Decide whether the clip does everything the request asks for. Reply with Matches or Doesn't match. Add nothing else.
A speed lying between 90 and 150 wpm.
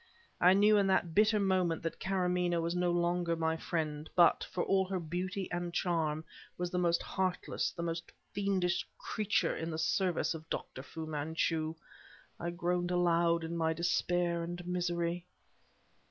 Doesn't match